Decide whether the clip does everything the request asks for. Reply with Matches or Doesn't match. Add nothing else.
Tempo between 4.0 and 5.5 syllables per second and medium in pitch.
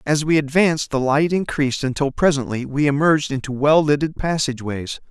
Doesn't match